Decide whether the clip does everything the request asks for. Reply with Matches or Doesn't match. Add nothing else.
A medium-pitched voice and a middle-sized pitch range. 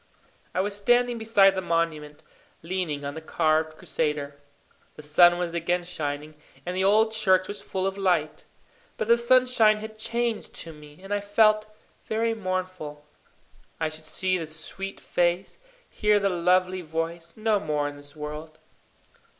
Matches